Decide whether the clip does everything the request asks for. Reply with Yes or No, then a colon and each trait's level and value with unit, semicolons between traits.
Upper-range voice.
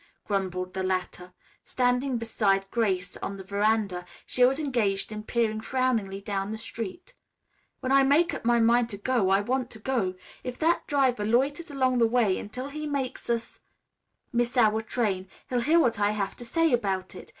Yes: high, 230 Hz